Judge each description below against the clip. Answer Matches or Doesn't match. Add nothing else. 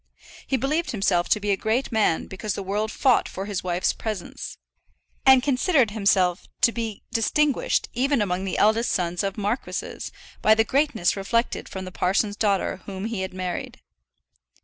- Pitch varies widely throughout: Doesn't match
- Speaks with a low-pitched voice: Doesn't match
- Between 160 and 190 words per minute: Matches